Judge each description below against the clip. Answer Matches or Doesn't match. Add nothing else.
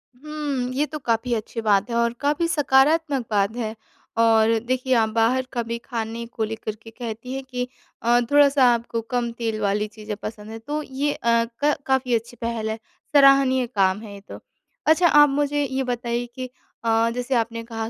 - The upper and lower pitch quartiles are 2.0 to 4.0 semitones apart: Matches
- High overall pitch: Matches